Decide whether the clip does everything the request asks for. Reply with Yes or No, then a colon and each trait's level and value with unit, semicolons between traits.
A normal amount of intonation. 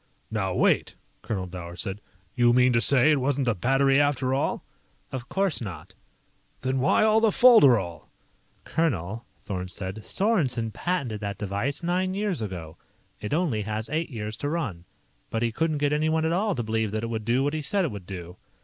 No: wide, 6.8 semitones